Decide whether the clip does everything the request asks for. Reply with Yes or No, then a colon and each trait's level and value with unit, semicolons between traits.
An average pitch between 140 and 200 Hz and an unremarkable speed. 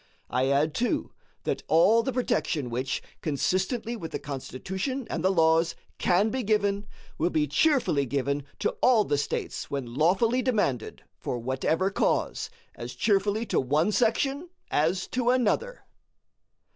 Yes: medium, 185 Hz; average, 145 wpm